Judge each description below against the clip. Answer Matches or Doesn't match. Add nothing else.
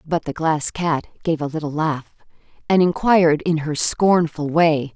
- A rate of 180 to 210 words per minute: Doesn't match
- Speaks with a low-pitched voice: Doesn't match